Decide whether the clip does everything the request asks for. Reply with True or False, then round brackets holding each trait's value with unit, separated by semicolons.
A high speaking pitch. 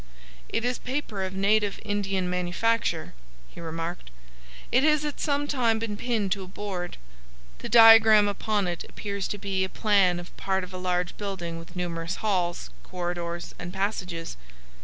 True (195 Hz)